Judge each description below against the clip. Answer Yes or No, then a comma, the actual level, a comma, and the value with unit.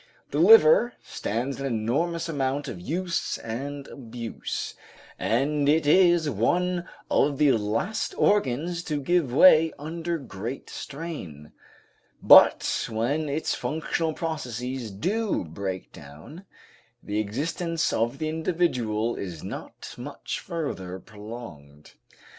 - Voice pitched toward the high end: No, medium, 140 Hz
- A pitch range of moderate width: No, wide, 6.7 semitones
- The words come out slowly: Yes, slow, 115 wpm